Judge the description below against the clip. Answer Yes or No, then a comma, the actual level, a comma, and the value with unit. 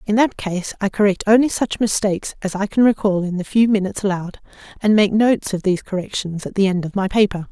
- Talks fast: Yes, fast, 230 wpm